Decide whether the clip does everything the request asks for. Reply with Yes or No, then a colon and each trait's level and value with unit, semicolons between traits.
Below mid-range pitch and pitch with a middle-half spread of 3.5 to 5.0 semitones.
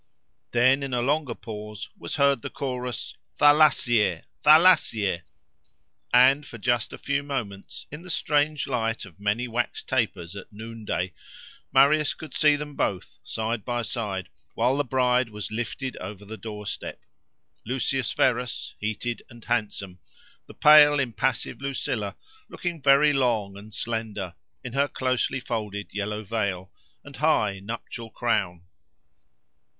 Yes: low, 120 Hz; average, 4.7 semitones